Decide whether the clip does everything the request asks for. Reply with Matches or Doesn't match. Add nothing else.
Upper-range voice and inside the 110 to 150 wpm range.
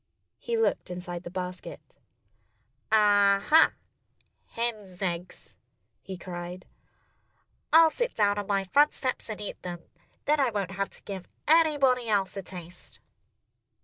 Matches